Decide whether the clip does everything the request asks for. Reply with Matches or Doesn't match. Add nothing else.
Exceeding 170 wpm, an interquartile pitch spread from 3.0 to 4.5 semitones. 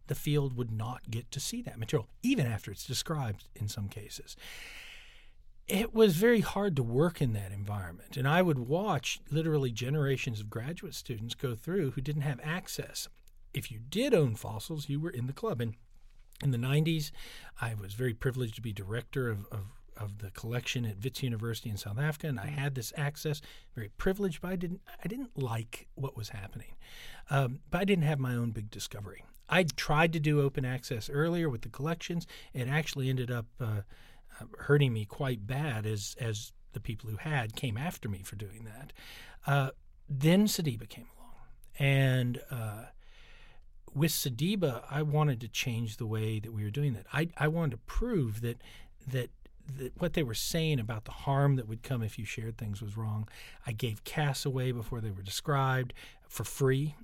Doesn't match